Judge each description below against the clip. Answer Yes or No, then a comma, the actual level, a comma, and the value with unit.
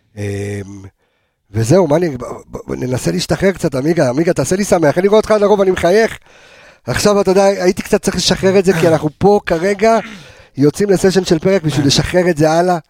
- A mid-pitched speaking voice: Yes, medium, 180 Hz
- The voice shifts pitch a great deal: No, average, 4.5 semitones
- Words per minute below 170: No, fast, 215 wpm